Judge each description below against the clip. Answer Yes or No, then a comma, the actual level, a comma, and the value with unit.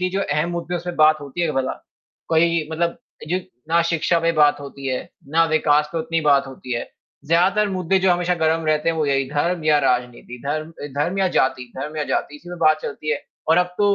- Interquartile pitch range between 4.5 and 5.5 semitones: No, average, 2.9 semitones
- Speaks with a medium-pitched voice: Yes, medium, 160 Hz